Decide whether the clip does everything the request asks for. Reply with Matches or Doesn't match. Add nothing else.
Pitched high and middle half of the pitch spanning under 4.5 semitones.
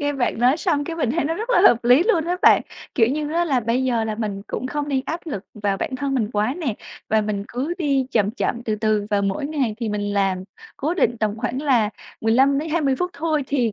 Doesn't match